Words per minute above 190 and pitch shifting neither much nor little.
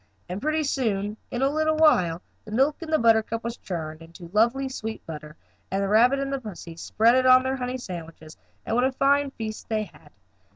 No: fast, 205 wpm; wide, 6.1 semitones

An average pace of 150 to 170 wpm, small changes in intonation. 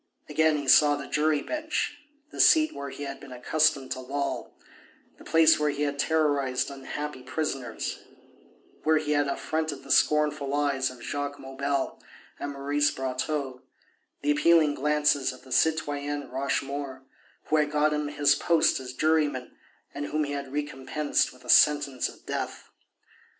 Yes: average, 155 wpm; narrow, 1.7 semitones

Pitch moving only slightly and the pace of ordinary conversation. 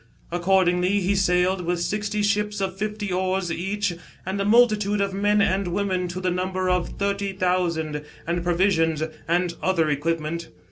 Yes: narrow, 2.3 semitones; average, 155 wpm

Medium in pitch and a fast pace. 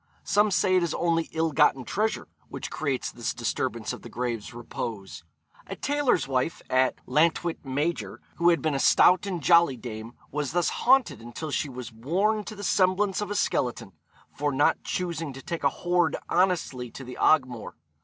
No: medium, 160 Hz; average, 180 wpm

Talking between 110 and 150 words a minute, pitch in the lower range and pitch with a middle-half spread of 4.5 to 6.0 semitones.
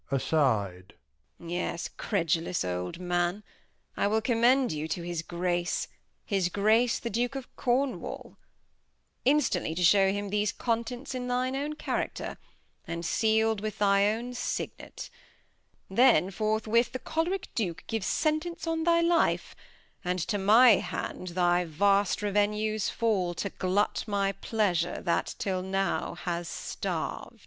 No: slow, 135 wpm; high, 205 Hz; average, 5.1 semitones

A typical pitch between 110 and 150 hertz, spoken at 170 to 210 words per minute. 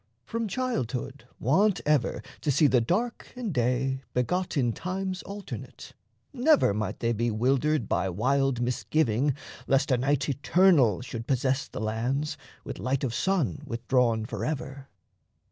No: low, 135 Hz; average, 140 wpm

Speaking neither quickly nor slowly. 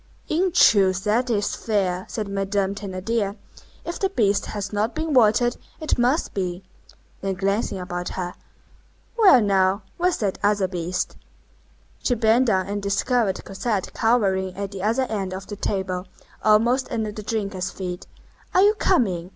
Yes: average, 155 wpm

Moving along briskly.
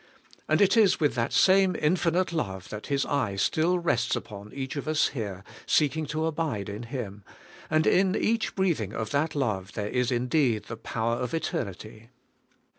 No: average, 175 wpm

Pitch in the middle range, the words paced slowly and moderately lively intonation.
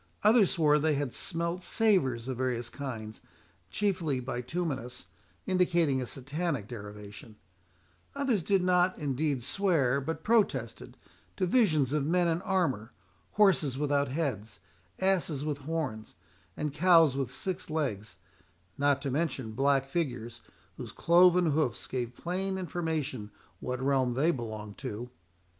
No: medium, 145 Hz; slow, 130 wpm; wide, 5.7 semitones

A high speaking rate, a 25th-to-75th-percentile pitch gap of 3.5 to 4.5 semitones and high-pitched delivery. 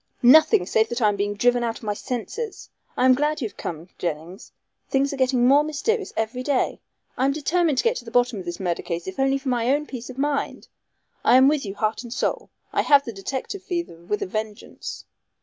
No: fast, 235 wpm; average, 5.0 semitones; high, 245 Hz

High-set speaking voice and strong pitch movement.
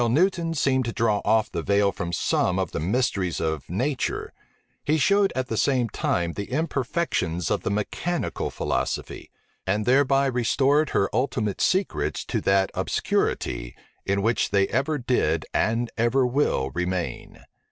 No: low, 115 Hz; wide, 6.1 semitones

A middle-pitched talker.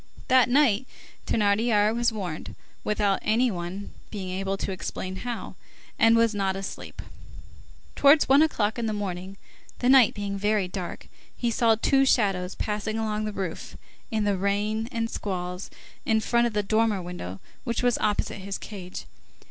No: high, 210 Hz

